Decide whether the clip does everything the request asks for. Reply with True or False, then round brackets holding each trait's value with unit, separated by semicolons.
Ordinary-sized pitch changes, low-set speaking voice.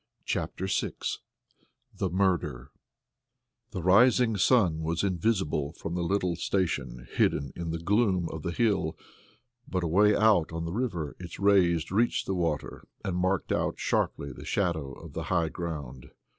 True (3.4 semitones; 90 Hz)